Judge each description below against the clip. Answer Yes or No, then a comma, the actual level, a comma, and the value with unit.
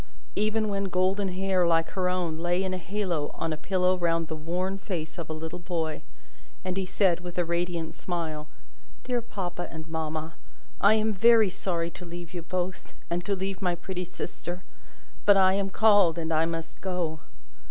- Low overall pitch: No, medium, 180 Hz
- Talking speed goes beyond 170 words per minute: Yes, average, 185 wpm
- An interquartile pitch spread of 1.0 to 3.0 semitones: Yes, narrow, 2.5 semitones